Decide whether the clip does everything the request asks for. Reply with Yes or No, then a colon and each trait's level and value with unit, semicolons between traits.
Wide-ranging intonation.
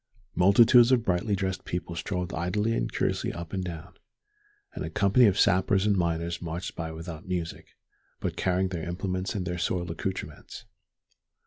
No: narrow, 2.4 semitones